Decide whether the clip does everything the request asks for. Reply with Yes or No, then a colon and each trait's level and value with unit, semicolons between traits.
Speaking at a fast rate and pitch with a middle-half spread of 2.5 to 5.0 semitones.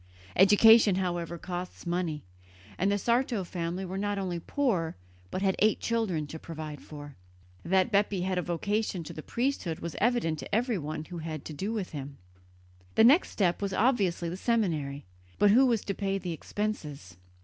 No: average, 180 wpm; average, 4.1 semitones